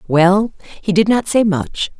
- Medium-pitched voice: No, high, 195 Hz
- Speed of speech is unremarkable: Yes, average, 180 wpm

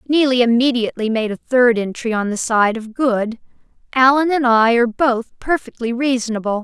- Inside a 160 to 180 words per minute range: Yes, average, 165 wpm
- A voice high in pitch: Yes, high, 240 Hz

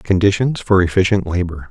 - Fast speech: No, average, 140 wpm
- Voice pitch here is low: Yes, very low, 95 Hz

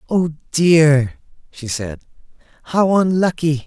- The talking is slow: Yes, slow, 100 wpm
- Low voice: No, medium, 155 Hz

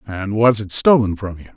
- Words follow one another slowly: No, fast, 230 wpm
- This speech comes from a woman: No, male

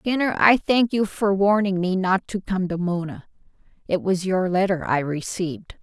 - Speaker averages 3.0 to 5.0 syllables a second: Yes, 4.6 syllables/s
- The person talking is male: No, female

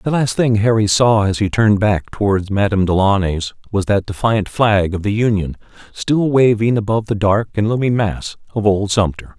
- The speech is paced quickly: No, average, 190 wpm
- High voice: No, low, 105 Hz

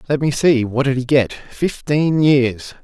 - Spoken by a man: Yes, male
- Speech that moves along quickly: No, average, 170 wpm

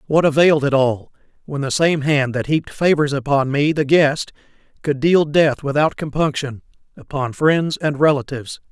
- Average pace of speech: Yes, average, 165 wpm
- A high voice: No, medium, 145 Hz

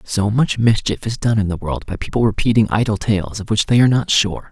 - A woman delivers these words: No, male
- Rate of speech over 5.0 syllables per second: Yes, 5.7 syllables/s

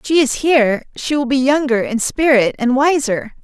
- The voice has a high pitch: Yes, very high, 265 Hz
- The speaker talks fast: Yes, fast, 210 wpm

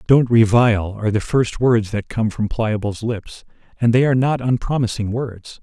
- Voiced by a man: Yes, male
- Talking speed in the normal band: Yes, average, 180 wpm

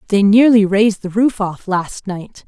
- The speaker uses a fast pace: No, average, 195 wpm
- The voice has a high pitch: Yes, high, 205 Hz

